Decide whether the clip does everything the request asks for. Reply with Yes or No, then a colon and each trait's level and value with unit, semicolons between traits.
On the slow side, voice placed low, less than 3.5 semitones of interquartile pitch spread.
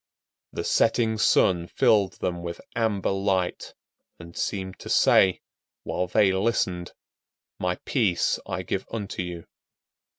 Yes: slow, 125 wpm; very low, 95 Hz; average, 3.0 semitones